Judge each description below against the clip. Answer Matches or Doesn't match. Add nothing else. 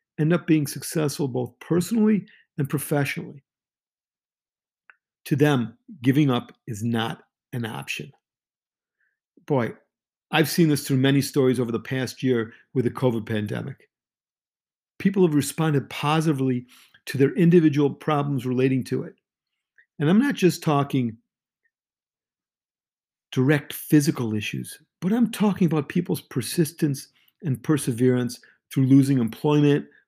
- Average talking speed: Doesn't match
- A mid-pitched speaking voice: Matches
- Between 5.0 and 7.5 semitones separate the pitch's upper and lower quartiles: Doesn't match